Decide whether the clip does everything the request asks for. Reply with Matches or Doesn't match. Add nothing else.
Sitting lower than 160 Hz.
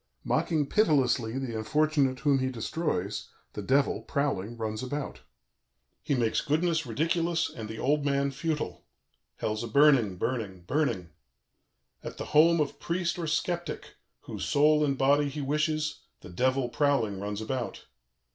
Matches